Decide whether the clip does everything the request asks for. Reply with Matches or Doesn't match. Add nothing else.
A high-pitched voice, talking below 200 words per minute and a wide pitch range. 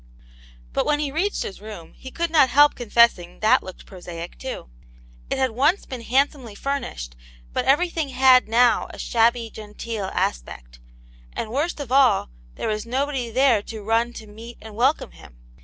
Doesn't match